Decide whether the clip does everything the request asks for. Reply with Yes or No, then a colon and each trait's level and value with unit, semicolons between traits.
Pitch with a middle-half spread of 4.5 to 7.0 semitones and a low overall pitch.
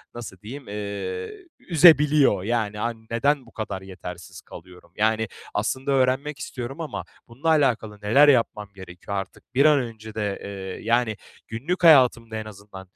Yes: average, 5.0 semitones; low, 115 Hz